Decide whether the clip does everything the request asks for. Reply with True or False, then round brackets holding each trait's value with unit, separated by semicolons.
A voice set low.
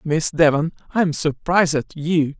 False (160 Hz)